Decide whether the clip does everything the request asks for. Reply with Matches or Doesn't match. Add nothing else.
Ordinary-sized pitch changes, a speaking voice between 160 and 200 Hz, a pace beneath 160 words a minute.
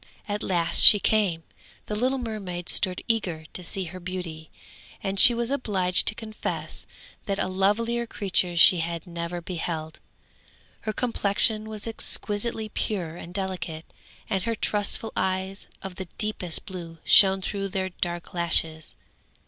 Matches